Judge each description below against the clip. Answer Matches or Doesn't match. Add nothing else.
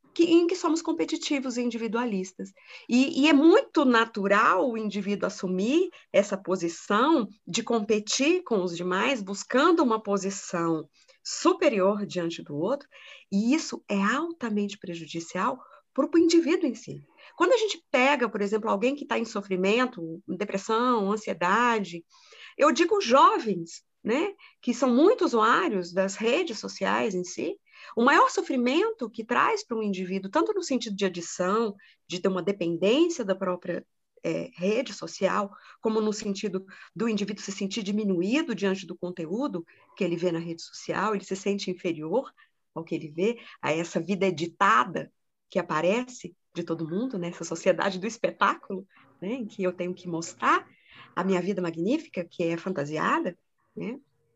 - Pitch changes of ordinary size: Doesn't match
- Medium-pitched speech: Doesn't match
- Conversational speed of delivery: Matches